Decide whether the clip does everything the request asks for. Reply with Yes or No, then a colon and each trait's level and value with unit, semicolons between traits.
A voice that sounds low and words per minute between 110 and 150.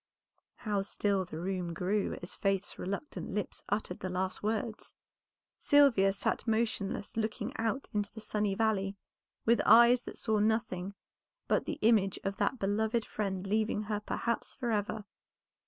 No: high, 210 Hz; average, 145 wpm